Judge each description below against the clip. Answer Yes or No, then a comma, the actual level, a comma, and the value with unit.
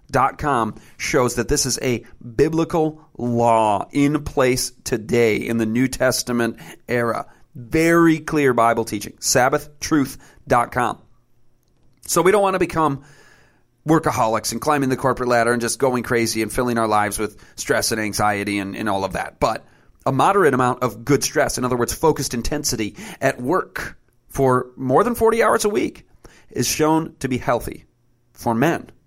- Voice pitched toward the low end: Yes, low, 125 Hz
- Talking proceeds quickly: No, average, 165 wpm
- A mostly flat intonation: No, average, 4.2 semitones